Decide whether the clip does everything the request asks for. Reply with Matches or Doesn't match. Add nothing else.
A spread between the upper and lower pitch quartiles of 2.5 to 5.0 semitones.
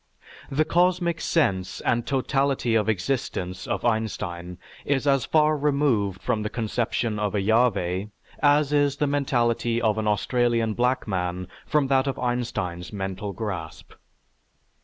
Doesn't match